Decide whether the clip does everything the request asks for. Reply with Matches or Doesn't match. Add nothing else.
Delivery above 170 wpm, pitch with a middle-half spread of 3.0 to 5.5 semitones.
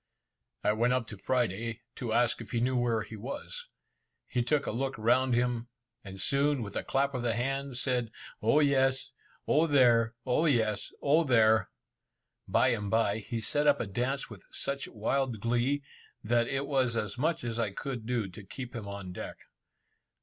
Matches